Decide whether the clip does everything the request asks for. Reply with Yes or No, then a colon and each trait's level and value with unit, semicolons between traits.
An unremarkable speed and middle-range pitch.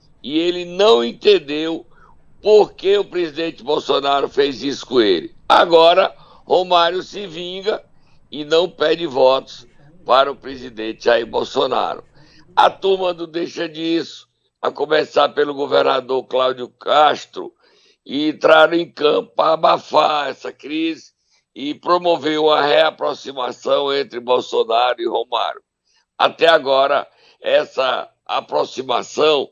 No: slow, 115 wpm; medium, 165 Hz